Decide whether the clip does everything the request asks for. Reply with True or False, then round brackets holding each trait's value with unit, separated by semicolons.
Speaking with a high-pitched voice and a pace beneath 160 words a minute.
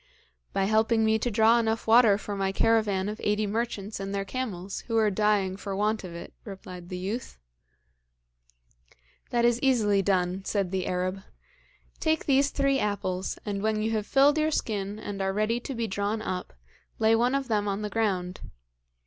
False (210 Hz; 185 wpm)